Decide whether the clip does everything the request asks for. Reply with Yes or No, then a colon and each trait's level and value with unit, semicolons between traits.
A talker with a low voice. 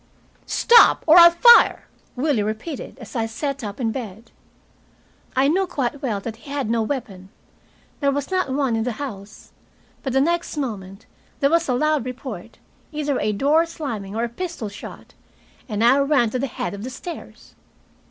No: very high, 260 Hz